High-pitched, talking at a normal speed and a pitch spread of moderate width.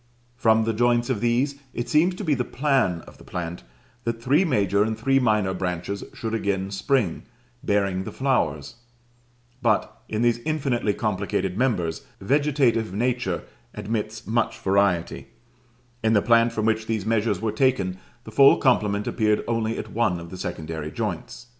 No: low, 110 Hz; average, 160 wpm; average, 3.7 semitones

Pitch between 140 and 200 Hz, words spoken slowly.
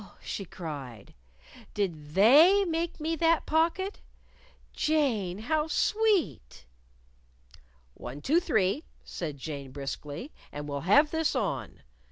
No: high, 220 Hz; slow, 110 wpm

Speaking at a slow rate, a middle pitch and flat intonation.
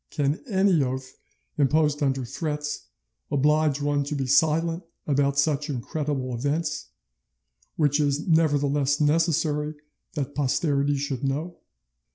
Yes: slow, 120 wpm; medium, 145 Hz; narrow, 1.9 semitones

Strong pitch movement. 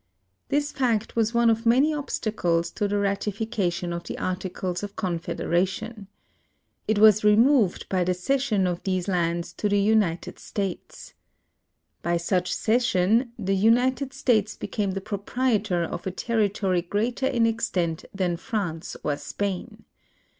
No: average, 4.0 semitones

